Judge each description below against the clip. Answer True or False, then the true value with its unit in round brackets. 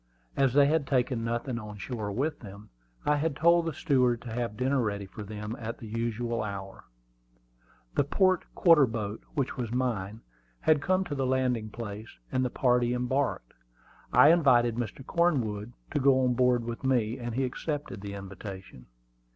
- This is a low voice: True (120 Hz)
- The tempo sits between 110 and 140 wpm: False (175 wpm)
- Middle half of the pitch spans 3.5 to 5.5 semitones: True (4.0 semitones)